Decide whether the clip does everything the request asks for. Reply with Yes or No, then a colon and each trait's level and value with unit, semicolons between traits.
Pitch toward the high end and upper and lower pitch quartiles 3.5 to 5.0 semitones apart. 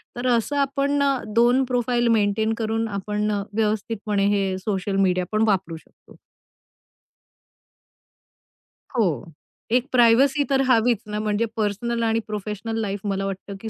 No: high, 220 Hz; average, 3.0 semitones